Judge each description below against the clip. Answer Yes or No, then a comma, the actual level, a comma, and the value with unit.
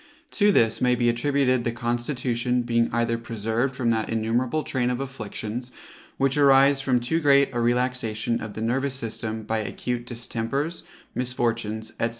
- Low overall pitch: Yes, low, 120 Hz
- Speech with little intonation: Yes, narrow, 2.2 semitones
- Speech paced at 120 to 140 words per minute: No, average, 155 wpm